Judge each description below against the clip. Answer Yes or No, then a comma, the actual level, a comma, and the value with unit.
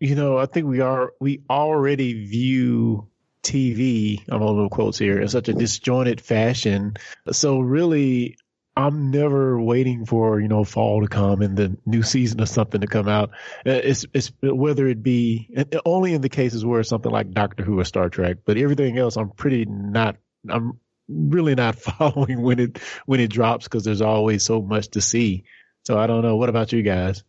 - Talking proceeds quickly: No, average, 195 wpm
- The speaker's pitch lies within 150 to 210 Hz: No, low, 115 Hz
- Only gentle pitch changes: No, average, 3.6 semitones